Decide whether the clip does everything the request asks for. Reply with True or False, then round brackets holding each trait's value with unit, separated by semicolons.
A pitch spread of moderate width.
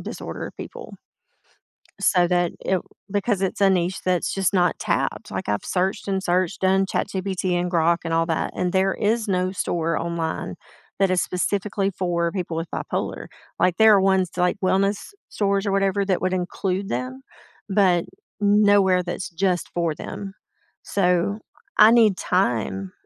False (2.0 semitones)